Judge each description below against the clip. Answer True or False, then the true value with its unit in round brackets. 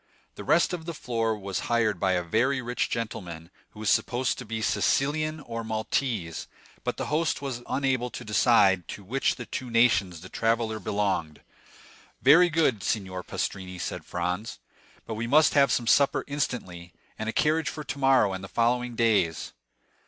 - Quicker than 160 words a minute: True (175 wpm)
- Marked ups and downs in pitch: True (5.7 semitones)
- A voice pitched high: False (115 Hz)